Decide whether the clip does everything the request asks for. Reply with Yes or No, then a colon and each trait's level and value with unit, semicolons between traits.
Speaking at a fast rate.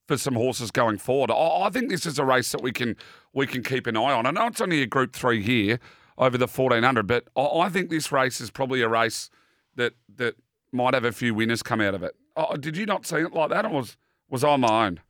Yes: fast, 260 wpm